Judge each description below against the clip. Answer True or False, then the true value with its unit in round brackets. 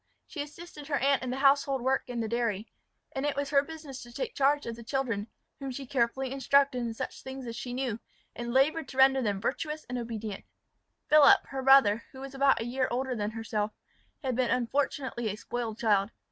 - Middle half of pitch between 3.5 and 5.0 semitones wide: False (2.9 semitones)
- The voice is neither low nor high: False (260 Hz)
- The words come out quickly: True (210 wpm)